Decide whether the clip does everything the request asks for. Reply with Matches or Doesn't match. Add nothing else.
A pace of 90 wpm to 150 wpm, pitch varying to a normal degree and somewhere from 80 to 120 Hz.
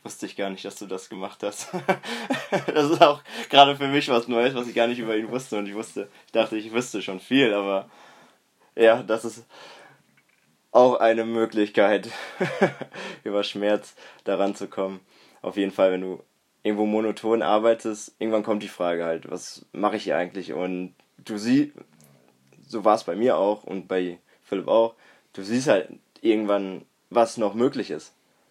Doesn't match